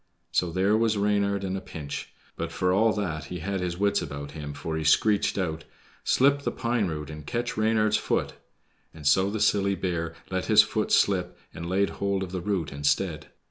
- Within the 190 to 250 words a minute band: Yes, average, 200 wpm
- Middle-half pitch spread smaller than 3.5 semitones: No, average, 4.2 semitones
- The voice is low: Yes, very low, 95 Hz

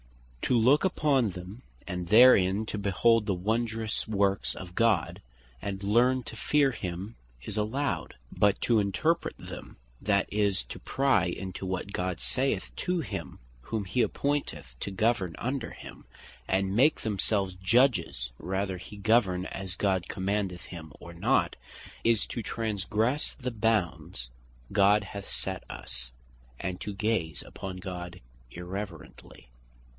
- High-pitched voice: No, low, 100 Hz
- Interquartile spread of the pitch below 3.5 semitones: No, average, 3.8 semitones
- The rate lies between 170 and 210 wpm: No, average, 140 wpm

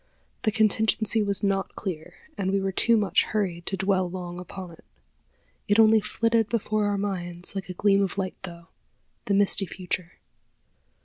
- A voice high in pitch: Yes, high, 195 Hz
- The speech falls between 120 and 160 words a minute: No, average, 170 wpm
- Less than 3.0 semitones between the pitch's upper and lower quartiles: Yes, narrow, 2.5 semitones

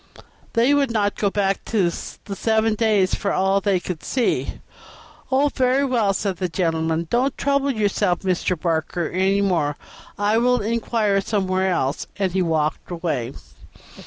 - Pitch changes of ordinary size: Yes, average, 4.1 semitones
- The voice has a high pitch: Yes, high, 195 Hz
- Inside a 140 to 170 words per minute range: Yes, average, 155 wpm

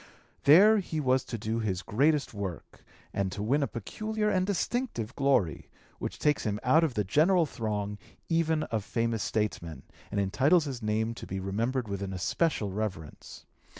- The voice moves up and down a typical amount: No, wide, 7.0 semitones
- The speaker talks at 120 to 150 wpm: No, average, 170 wpm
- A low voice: Yes, low, 115 Hz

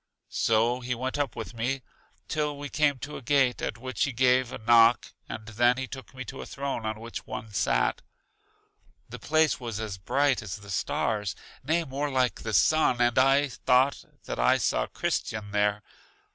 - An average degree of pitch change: Yes, average, 3.7 semitones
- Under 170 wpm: No, average, 185 wpm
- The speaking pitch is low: Yes, low, 125 Hz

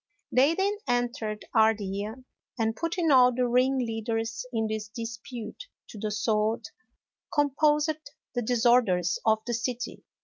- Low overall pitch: No, high, 235 Hz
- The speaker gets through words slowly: Yes, slow, 125 wpm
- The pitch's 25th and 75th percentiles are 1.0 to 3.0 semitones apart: Yes, narrow, 2.6 semitones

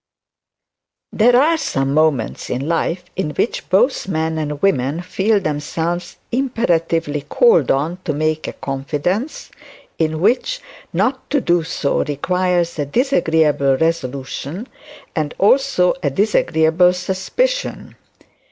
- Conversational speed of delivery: No, slow, 115 wpm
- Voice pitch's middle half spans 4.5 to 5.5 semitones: Yes, average, 4.9 semitones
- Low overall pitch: No, medium, 170 Hz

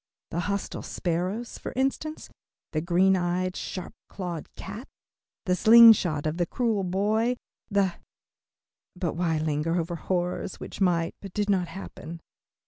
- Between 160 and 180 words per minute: No, average, 140 wpm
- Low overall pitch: No, medium, 185 Hz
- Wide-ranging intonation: No, average, 2.9 semitones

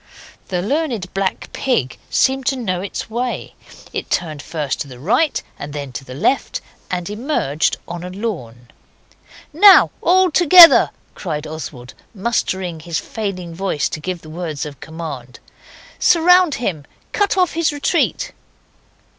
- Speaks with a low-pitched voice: No, medium, 185 Hz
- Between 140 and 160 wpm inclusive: Yes, average, 145 wpm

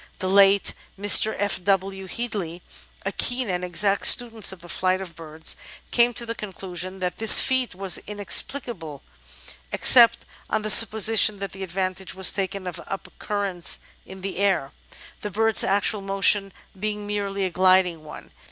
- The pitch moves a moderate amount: No, narrow, 2.1 semitones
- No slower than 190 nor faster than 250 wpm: No, average, 160 wpm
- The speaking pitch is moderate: No, high, 195 Hz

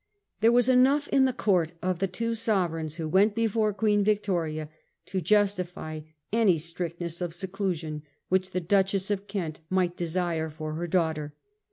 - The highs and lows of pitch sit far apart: No, average, 3.9 semitones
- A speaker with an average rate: Yes, average, 165 wpm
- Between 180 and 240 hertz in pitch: Yes, medium, 185 Hz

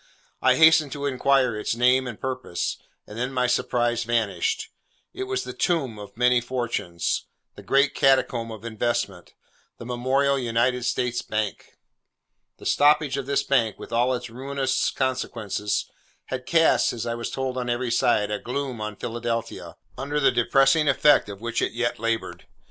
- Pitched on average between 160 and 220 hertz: No, low, 125 Hz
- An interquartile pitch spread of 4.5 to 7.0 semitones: No, average, 2.8 semitones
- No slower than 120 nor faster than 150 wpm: No, average, 165 wpm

